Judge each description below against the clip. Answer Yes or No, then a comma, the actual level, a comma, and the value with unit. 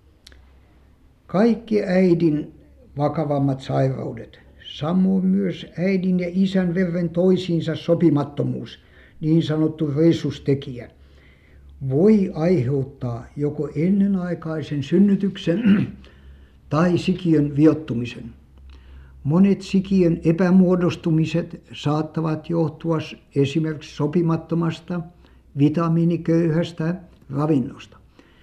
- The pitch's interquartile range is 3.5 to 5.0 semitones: Yes, average, 4.2 semitones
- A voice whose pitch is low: No, medium, 160 Hz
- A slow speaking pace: Yes, slow, 70 wpm